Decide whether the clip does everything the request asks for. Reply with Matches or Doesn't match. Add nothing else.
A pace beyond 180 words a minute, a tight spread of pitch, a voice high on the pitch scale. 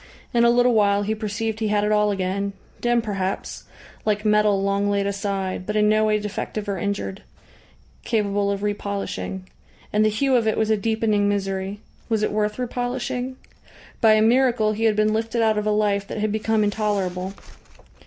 Matches